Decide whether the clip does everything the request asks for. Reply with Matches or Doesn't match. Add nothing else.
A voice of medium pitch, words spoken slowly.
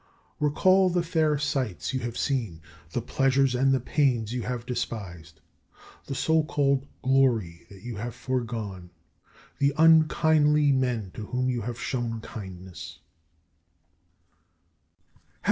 Doesn't match